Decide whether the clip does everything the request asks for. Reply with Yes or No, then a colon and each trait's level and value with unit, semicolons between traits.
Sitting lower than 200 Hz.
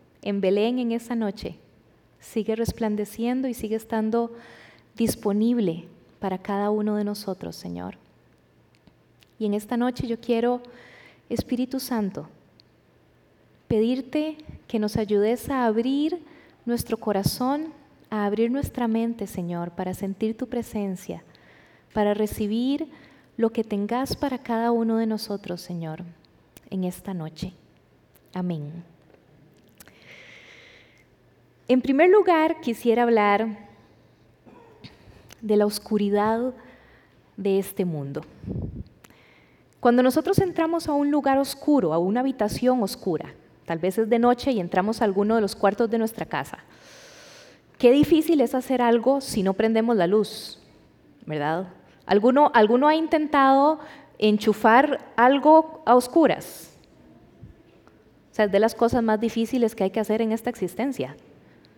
No: high, 225 Hz